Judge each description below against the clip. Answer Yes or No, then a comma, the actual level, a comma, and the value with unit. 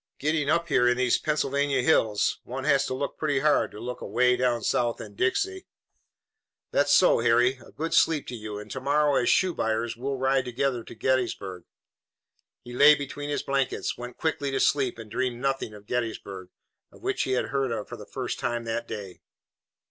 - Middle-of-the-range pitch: No, low, 130 Hz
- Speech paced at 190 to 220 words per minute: Yes, average, 195 wpm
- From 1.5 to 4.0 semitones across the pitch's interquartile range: Yes, average, 3.3 semitones